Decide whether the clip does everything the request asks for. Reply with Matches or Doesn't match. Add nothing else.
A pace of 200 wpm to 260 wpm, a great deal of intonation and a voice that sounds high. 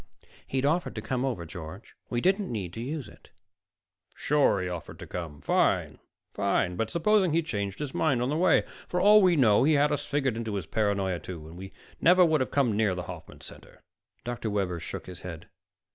Doesn't match